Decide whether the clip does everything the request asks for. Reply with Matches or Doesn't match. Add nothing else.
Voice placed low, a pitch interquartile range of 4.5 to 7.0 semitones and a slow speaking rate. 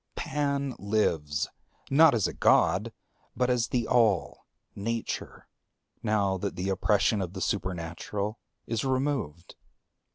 Matches